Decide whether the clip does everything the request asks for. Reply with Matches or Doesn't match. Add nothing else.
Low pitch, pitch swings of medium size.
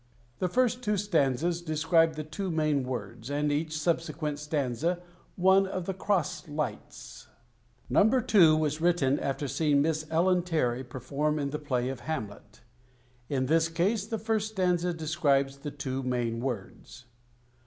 Doesn't match